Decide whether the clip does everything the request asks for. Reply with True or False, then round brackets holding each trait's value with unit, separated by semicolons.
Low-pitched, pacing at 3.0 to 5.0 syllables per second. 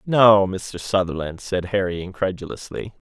True (95 Hz; 4.6 syllables/s)